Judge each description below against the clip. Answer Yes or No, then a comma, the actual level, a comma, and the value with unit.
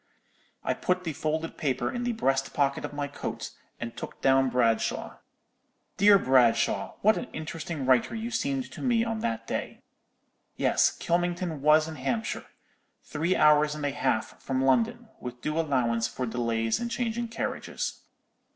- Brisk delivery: No, average, 160 wpm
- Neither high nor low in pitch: Yes, medium, 150 Hz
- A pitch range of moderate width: No, wide, 8.1 semitones